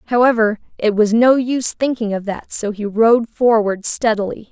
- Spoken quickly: No, average, 175 wpm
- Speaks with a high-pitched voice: Yes, high, 225 Hz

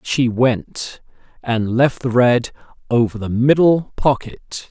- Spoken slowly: Yes, slow, 130 wpm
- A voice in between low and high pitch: No, low, 125 Hz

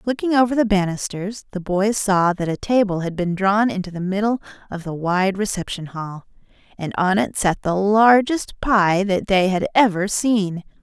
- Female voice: Yes, female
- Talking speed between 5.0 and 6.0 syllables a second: No, 4.6 syllables/s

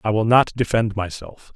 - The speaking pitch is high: No, low, 110 Hz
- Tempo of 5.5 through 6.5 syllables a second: No, 5.0 syllables/s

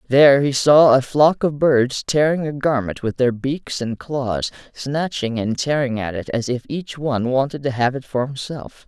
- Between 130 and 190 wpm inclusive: No, fast, 205 wpm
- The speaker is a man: Yes, male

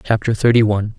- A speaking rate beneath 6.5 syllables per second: No, 6.8 syllables/s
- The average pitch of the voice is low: Yes, low, 110 Hz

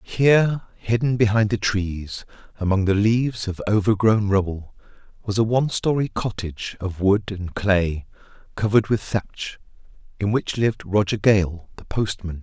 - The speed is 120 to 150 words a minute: Yes, average, 145 wpm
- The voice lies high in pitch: No, low, 105 Hz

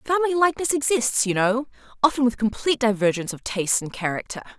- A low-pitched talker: No, high, 245 Hz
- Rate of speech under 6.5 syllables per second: No, 7.0 syllables/s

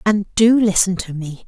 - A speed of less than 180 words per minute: No, fast, 205 wpm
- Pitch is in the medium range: No, high, 195 Hz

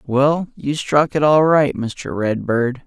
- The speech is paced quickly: No, average, 170 wpm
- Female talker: No, male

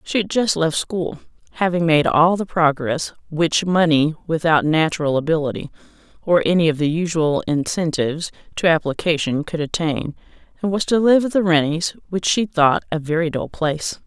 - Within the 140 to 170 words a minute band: Yes, average, 165 wpm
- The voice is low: No, medium, 165 Hz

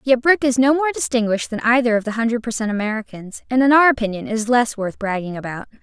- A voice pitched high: Yes, high, 235 Hz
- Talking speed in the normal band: No, fast, 225 wpm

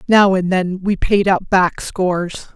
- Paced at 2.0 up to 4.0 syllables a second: Yes, 3.9 syllables/s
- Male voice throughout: No, female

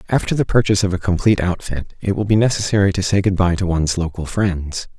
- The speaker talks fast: Yes, fast, 215 wpm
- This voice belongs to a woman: No, male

